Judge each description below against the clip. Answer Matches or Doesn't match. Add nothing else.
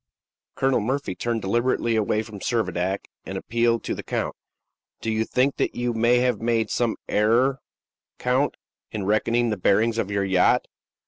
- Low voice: Matches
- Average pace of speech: Matches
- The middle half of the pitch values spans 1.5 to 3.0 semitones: Matches